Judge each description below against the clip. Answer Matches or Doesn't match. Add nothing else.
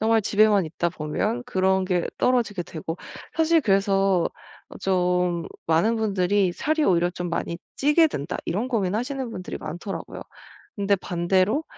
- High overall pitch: Matches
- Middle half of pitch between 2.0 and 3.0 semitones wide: Doesn't match